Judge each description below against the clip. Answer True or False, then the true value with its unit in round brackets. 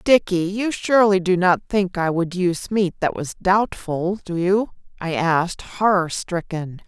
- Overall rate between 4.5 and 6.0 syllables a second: False (4.3 syllables/s)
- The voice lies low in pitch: False (185 Hz)